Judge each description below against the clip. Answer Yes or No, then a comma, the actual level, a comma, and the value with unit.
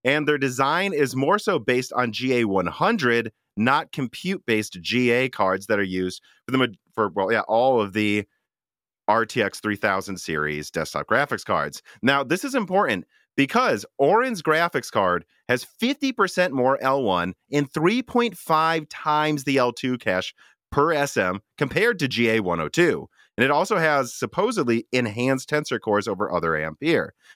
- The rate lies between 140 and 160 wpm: Yes, average, 145 wpm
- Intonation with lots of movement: Yes, wide, 6.6 semitones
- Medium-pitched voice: No, low, 125 Hz